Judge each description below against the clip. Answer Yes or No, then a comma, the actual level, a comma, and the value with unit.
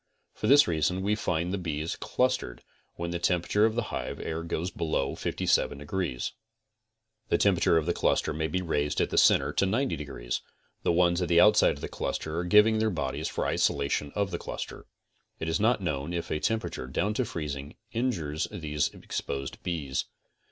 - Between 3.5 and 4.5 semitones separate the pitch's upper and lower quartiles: No, average, 4.9 semitones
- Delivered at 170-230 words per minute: Yes, average, 185 wpm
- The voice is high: No, very low, 85 Hz